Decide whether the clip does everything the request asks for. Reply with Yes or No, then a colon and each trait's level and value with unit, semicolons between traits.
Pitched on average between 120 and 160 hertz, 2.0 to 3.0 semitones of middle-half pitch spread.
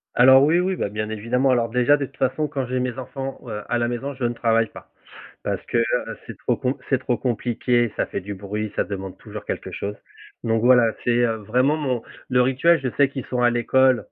Yes: low, 125 Hz; narrow, 2.6 semitones